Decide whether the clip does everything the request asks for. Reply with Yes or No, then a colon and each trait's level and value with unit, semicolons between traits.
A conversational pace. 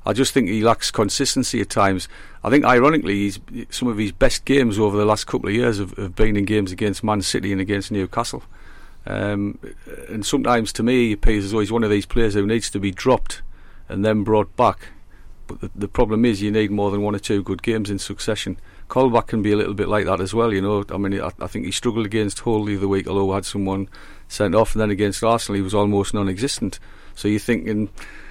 No: fast, 240 wpm